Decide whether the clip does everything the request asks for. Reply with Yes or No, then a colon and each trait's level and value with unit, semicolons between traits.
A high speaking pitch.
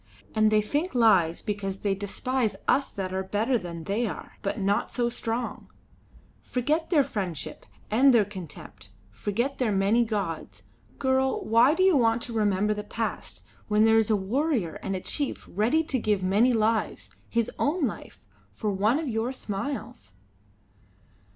Yes: high, 220 Hz